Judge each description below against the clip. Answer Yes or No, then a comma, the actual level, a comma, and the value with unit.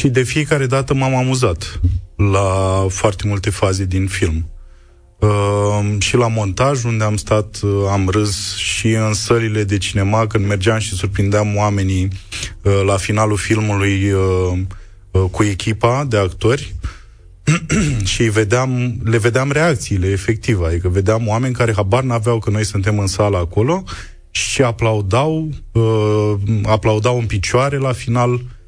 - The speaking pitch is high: No, low, 105 Hz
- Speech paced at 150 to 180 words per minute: No, average, 140 wpm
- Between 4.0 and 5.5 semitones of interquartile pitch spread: No, average, 3.2 semitones